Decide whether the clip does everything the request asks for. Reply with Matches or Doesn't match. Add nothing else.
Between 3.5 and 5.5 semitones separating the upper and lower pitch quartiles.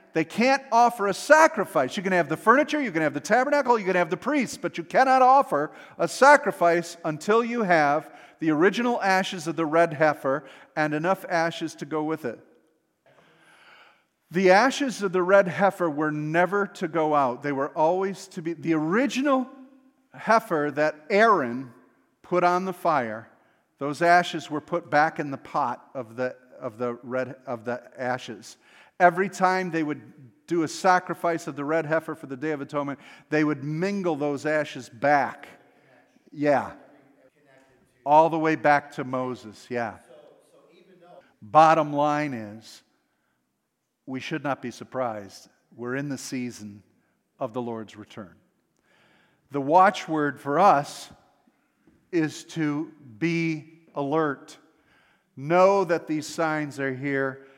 Matches